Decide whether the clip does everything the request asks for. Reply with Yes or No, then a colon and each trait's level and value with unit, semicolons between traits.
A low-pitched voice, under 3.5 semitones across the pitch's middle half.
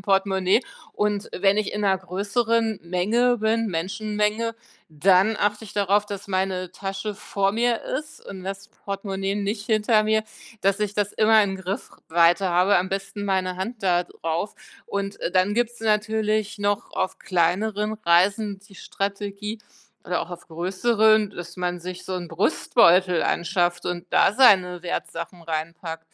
No: high, 195 Hz; narrow, 2.6 semitones